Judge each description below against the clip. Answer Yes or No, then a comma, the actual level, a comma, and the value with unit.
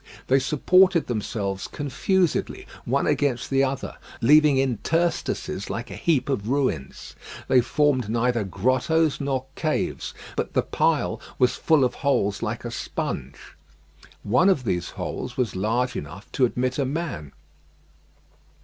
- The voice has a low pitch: Yes, low, 130 Hz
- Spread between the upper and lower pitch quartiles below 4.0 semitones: No, average, 4.3 semitones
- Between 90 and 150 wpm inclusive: Yes, slow, 135 wpm